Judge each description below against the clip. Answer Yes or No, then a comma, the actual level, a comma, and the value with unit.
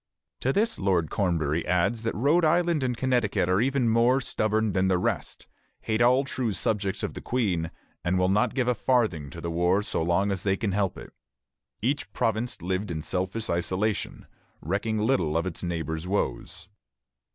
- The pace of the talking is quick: No, average, 180 wpm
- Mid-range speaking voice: No, low, 100 Hz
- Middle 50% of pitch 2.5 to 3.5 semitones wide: No, average, 5.2 semitones